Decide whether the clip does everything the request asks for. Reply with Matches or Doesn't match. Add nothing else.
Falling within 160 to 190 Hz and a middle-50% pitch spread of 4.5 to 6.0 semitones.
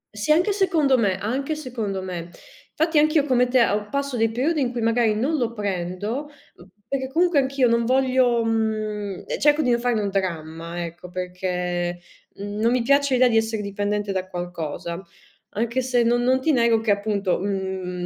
Doesn't match